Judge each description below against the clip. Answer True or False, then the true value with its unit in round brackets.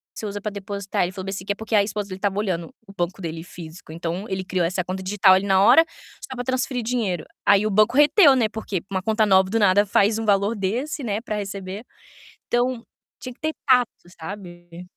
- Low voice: False (200 Hz)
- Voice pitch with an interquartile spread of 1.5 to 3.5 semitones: True (2.9 semitones)